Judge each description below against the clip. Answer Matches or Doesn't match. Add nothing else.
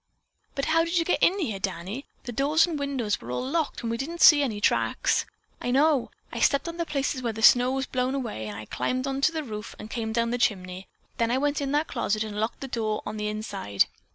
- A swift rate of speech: Matches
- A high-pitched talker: Matches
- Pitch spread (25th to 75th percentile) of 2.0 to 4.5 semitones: Doesn't match